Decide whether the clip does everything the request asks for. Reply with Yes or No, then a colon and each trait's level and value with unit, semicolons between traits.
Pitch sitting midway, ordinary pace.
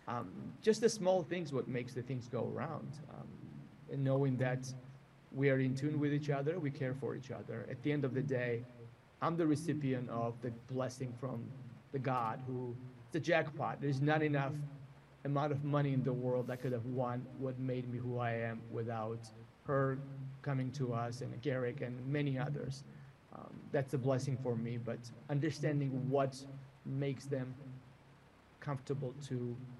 No: low, 130 Hz; average, 175 wpm